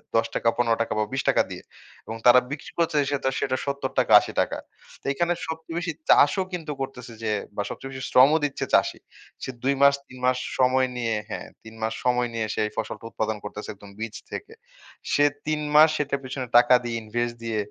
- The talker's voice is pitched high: No, low, 125 Hz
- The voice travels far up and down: No, average, 3.8 semitones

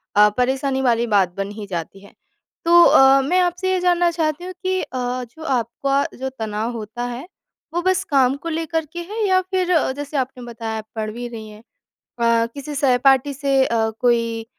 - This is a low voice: No, very high, 265 Hz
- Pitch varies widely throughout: Yes, wide, 5.9 semitones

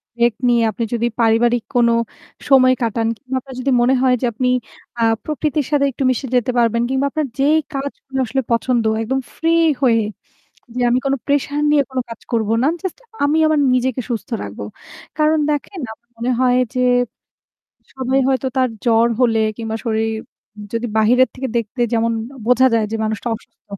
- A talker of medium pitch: No, very high, 250 Hz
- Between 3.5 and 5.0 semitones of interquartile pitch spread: No, average, 2.8 semitones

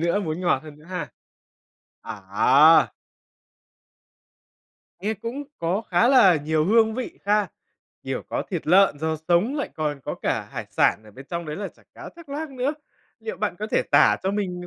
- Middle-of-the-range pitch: Yes, medium, 180 Hz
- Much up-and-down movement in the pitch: Yes, wide, 6.1 semitones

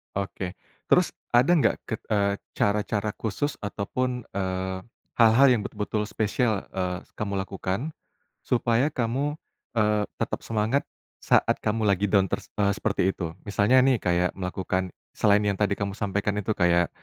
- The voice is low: Yes, low, 105 Hz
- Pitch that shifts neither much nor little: Yes, average, 3.0 semitones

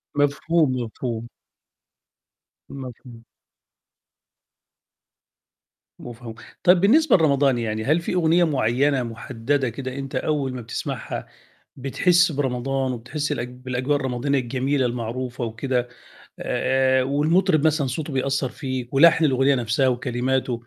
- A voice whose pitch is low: Yes, low, 130 Hz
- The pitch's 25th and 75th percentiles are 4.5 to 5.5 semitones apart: No, average, 2.9 semitones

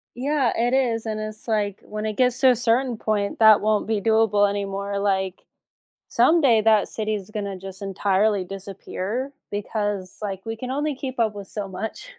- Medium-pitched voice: No, high, 215 Hz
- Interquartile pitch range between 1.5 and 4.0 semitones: Yes, narrow, 2.6 semitones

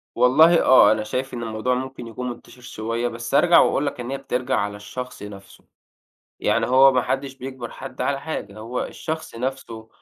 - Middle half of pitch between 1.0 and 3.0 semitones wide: Yes, average, 2.7 semitones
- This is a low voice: Yes, low, 125 Hz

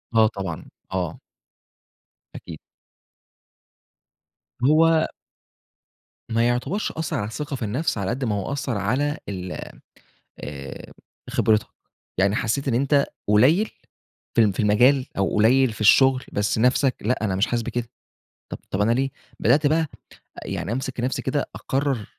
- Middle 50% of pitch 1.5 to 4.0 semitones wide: No, average, 4.7 semitones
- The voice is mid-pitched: No, low, 120 Hz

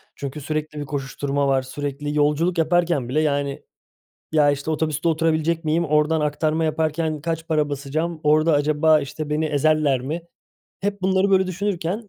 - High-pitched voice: No, medium, 155 Hz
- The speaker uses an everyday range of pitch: No, narrow, 2.1 semitones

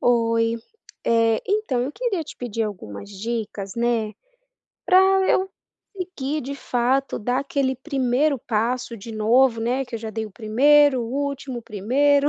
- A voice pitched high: Yes, high, 245 Hz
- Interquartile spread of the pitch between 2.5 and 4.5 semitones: Yes, average, 3.7 semitones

